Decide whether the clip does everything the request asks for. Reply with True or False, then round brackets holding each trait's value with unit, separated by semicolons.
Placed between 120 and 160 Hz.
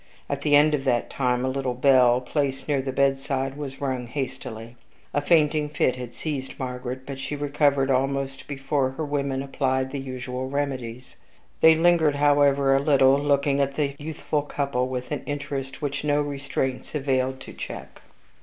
True (135 Hz)